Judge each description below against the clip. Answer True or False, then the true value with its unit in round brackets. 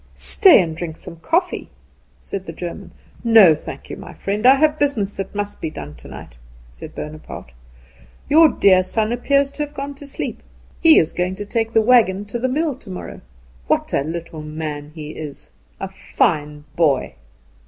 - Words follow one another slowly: False (175 wpm)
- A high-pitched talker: True (195 Hz)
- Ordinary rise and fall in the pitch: False (7.8 semitones)